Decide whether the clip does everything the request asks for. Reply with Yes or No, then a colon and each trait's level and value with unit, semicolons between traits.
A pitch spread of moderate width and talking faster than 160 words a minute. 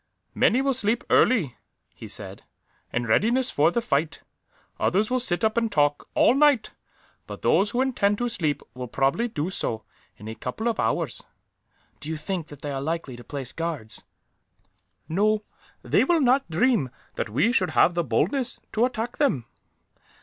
No: wide, 8.7 semitones; average, 170 wpm